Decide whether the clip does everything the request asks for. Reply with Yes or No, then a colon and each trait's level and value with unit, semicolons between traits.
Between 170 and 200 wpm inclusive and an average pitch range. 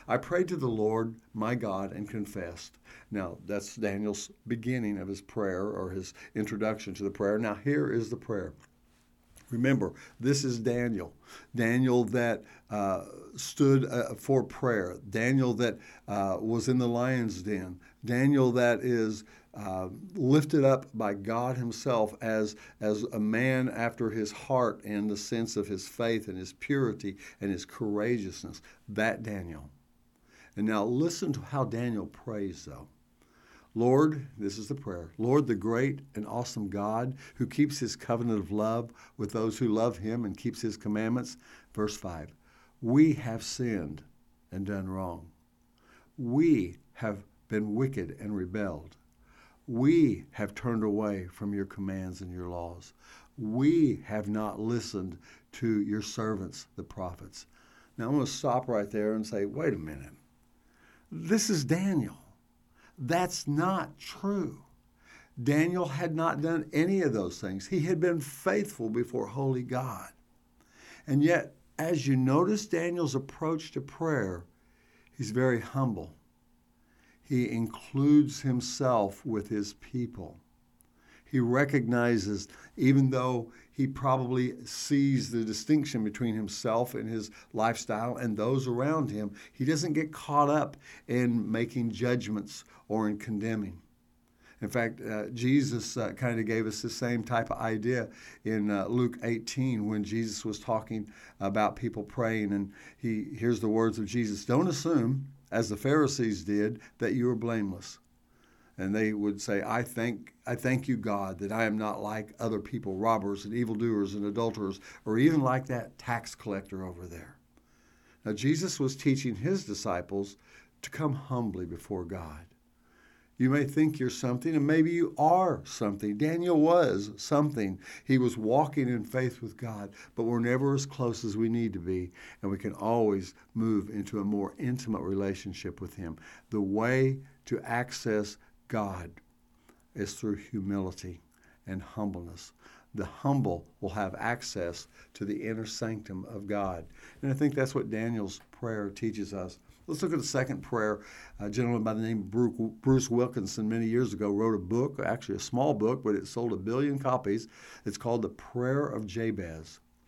No: average, 155 wpm; average, 3.9 semitones